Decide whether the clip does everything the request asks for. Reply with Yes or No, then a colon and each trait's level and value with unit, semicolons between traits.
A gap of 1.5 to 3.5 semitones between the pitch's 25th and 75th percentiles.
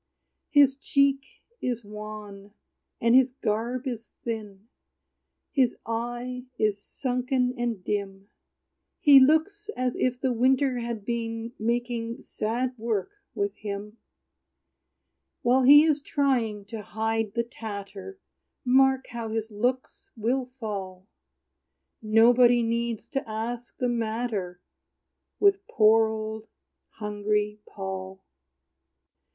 Yes: average, 3.1 semitones